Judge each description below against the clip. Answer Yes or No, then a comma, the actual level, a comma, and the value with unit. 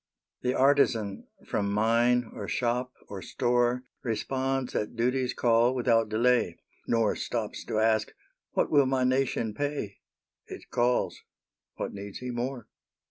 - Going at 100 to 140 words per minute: Yes, slow, 135 wpm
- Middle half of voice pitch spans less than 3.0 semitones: Yes, narrow, 2.5 semitones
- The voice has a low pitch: Yes, low, 120 Hz